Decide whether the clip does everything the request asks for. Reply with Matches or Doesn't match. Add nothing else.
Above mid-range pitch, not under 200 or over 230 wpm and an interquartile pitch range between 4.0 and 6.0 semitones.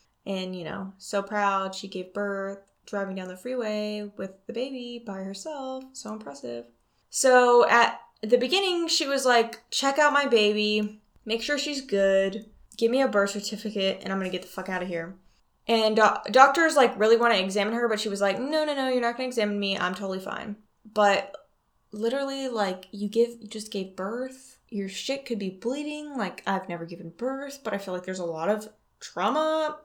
Matches